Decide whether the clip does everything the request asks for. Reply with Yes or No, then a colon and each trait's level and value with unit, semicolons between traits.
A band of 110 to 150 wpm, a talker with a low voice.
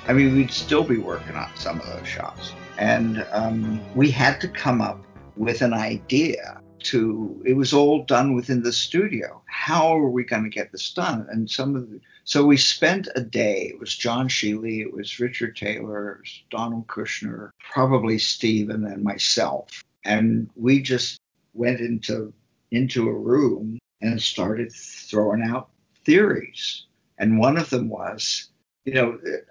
No: average, 165 wpm; low, 115 Hz